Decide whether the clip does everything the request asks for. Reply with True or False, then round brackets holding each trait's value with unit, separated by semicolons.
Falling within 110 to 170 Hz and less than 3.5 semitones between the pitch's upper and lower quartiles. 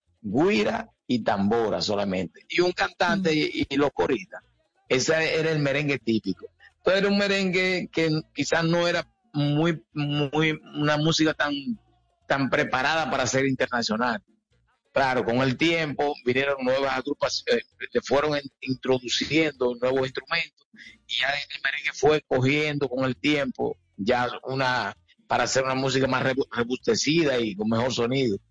False (140 Hz; 3.8 semitones)